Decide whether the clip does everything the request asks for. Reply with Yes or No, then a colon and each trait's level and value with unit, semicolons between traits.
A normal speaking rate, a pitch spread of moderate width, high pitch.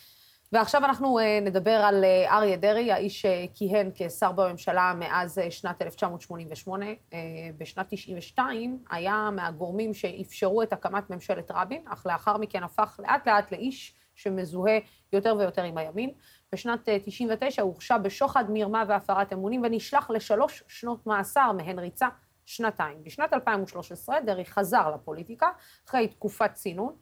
Yes: average, 125 wpm; average, 3.4 semitones; high, 205 Hz